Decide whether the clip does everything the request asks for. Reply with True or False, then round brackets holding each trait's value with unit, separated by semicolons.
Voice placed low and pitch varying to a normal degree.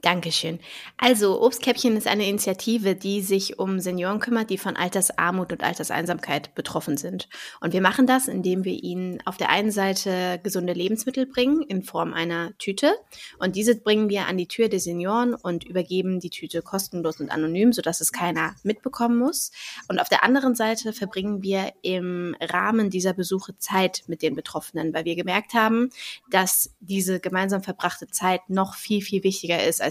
False (190 Hz; 3.2 semitones)